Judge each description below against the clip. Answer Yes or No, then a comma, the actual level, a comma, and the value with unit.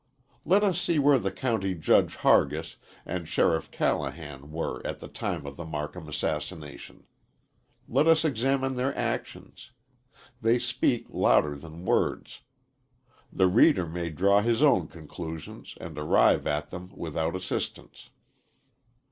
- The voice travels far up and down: Yes, wide, 7.9 semitones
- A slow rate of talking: Yes, slow, 130 wpm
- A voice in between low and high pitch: No, very low, 90 Hz